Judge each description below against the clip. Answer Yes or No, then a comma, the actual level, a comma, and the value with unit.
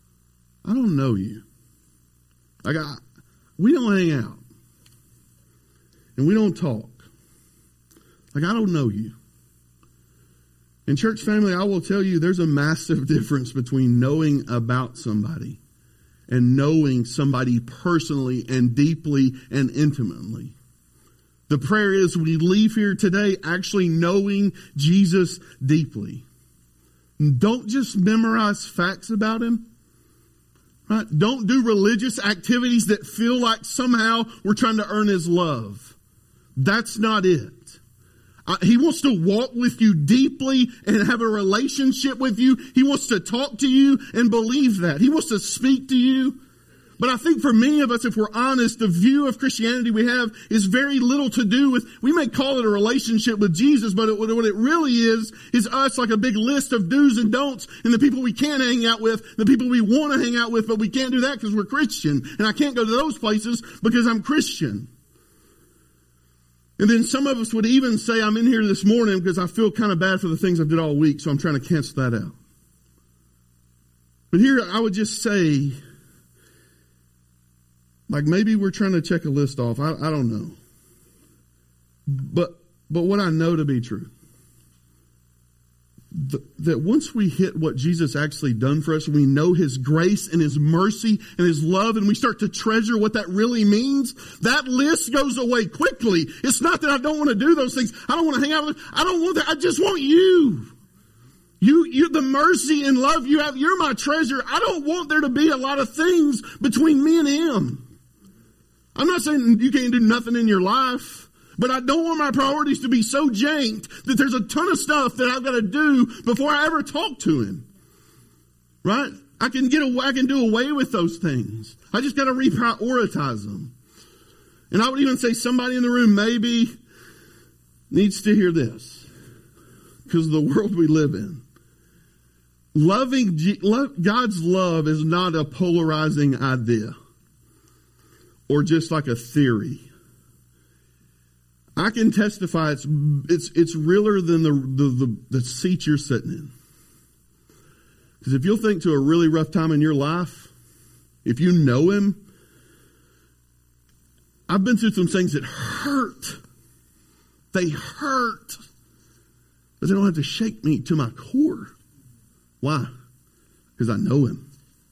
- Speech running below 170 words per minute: No, average, 175 wpm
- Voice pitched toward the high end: Yes, high, 195 Hz